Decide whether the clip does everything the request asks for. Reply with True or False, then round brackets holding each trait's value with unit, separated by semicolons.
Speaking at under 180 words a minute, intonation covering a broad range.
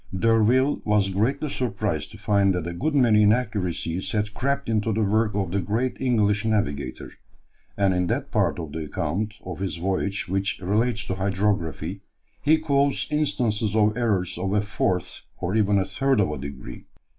False (170 wpm; 3.2 semitones)